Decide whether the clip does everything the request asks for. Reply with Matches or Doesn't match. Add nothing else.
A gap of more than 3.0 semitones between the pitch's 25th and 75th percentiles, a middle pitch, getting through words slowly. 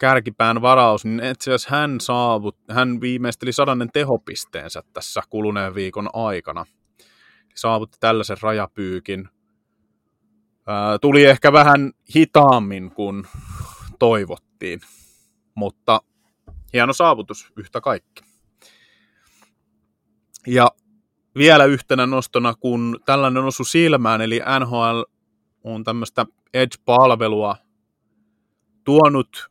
Doesn't match